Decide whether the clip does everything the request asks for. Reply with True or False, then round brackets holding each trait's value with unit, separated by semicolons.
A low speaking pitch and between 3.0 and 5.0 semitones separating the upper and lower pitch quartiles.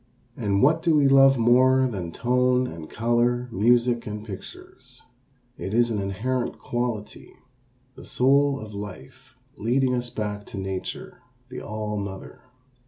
True (120 Hz; 3.6 semitones)